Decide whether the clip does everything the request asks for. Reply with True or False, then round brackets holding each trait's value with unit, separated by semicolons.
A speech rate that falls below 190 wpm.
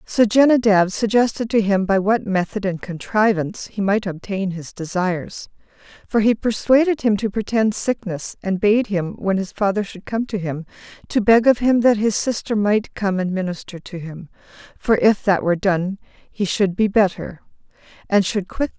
False (195 wpm)